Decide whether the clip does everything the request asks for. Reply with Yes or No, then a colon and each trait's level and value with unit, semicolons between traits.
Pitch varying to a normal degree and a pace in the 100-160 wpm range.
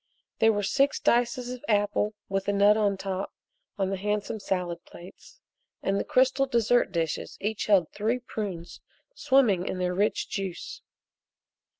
Yes: average, 3.5 semitones; average, 155 wpm